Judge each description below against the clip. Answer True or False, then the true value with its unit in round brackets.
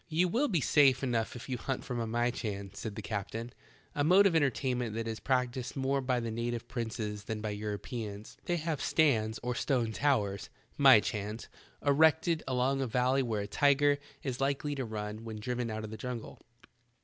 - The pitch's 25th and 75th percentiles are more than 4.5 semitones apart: False (3.9 semitones)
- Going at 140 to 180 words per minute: False (190 wpm)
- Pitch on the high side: False (125 Hz)